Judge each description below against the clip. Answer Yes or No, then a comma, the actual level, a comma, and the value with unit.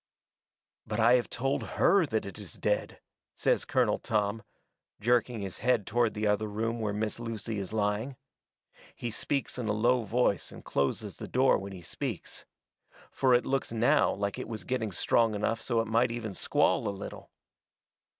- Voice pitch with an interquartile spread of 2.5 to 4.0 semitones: Yes, average, 2.8 semitones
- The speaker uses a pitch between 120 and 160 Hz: No, low, 110 Hz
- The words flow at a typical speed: Yes, average, 180 wpm